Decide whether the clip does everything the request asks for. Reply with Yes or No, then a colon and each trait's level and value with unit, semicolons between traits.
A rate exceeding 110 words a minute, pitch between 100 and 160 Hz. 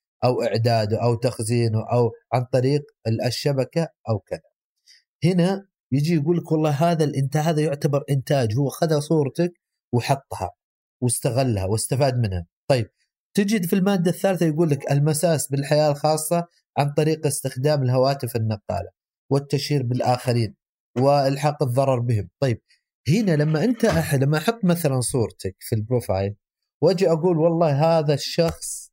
Yes: average, 130 wpm; medium, 140 Hz